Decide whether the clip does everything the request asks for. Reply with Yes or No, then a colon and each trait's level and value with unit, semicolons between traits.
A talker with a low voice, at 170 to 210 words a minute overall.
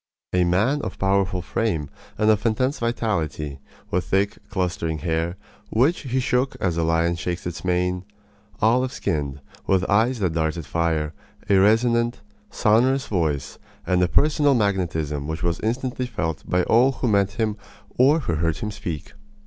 No: very low, 95 Hz; average, 155 wpm